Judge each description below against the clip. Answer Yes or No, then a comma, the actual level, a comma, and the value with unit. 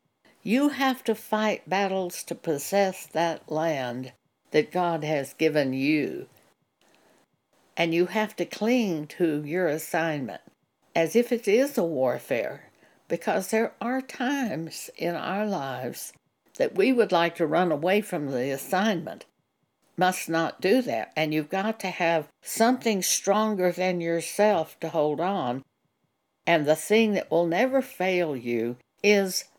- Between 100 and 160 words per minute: Yes, average, 140 wpm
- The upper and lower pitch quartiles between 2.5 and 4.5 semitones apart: No, average, 5.2 semitones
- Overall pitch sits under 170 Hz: No, medium, 180 Hz